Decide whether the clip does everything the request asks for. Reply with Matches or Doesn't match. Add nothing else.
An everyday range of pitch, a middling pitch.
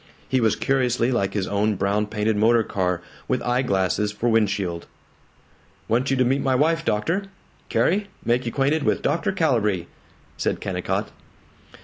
Doesn't match